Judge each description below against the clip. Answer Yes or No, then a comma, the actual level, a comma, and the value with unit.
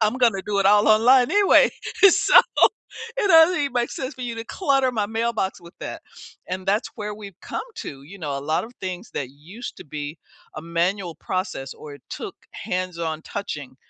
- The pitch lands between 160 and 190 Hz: No, high, 200 Hz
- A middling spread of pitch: No, wide, 6.2 semitones